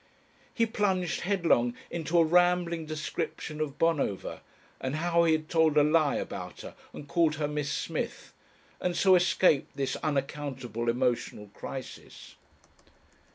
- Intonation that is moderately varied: Yes, average, 3.7 semitones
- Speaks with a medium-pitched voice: Yes, medium, 155 Hz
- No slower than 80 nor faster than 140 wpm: Yes, slow, 135 wpm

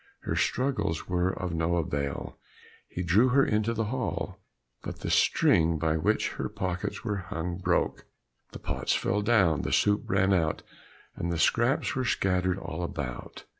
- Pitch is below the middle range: Yes, very low, 90 Hz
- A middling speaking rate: Yes, average, 165 wpm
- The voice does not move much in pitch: No, average, 4.0 semitones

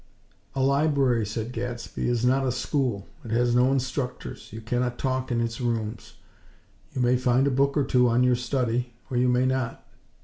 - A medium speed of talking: Yes, average, 190 wpm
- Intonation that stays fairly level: Yes, narrow, 1.6 semitones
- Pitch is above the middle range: No, low, 125 Hz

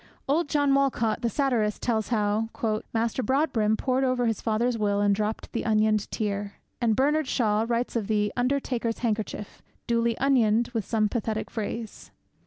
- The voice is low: No, high, 230 Hz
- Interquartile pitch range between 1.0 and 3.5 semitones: Yes, average, 2.8 semitones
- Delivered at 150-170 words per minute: Yes, average, 160 wpm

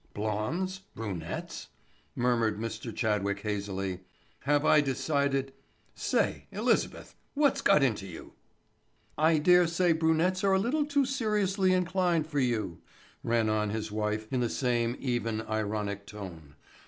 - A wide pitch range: Yes, wide, 8.0 semitones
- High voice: No, low, 120 Hz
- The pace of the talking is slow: Yes, slow, 125 wpm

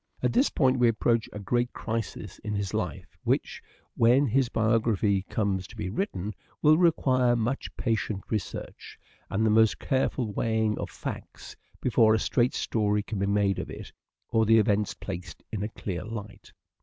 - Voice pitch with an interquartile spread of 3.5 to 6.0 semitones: No, average, 2.8 semitones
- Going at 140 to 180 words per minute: Yes, average, 170 wpm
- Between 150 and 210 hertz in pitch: No, low, 110 Hz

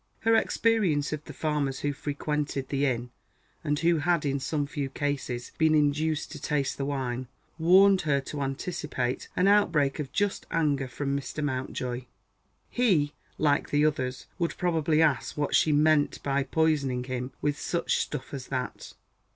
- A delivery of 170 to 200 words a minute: No, average, 160 wpm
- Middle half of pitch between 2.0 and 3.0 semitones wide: Yes, average, 2.7 semitones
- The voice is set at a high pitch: No, medium, 145 Hz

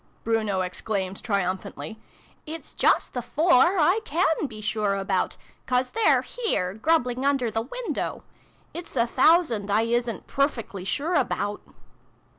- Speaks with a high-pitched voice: Yes, high, 240 Hz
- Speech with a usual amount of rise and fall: No, wide, 6.8 semitones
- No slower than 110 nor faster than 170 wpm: Yes, average, 140 wpm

